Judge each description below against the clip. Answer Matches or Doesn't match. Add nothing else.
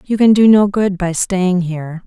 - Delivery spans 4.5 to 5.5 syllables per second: Matches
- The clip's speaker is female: Matches